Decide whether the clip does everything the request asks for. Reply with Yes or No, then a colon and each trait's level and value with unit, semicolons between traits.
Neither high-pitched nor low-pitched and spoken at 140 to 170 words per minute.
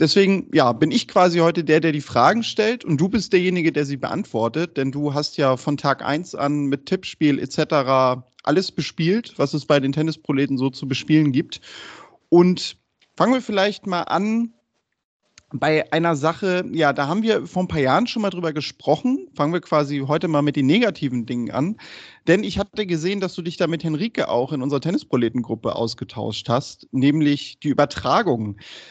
No: medium, 155 Hz; average, 185 wpm